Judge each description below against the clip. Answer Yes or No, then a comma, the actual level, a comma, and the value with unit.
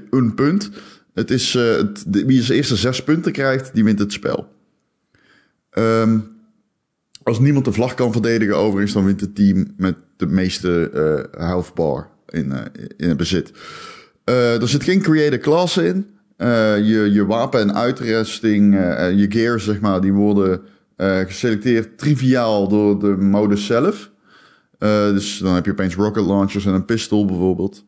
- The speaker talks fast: No, average, 170 wpm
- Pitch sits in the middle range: No, low, 105 Hz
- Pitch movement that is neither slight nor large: Yes, average, 3.4 semitones